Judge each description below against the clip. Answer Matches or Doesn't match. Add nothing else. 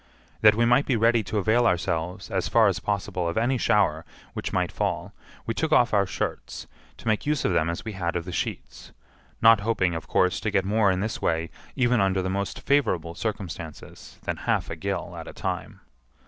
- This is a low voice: Matches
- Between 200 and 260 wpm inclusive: Matches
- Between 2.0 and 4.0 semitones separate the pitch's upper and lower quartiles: Doesn't match